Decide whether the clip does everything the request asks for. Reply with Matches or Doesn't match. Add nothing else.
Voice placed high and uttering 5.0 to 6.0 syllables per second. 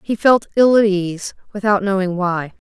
Doesn't match